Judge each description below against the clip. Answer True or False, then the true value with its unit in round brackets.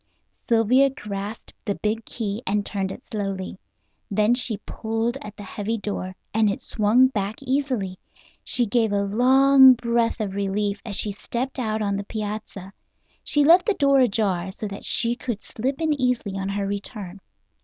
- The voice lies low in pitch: False (215 Hz)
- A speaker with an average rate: True (170 wpm)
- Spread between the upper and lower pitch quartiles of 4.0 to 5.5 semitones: False (3.5 semitones)